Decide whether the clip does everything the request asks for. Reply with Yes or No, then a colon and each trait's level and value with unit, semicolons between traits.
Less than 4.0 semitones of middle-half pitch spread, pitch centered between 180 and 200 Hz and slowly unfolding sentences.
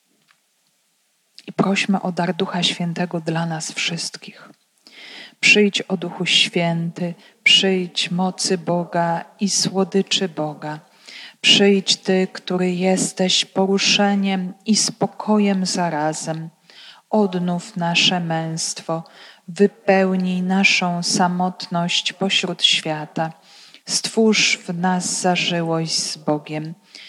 Yes: narrow, 2.5 semitones; medium, 185 Hz; slow, 90 wpm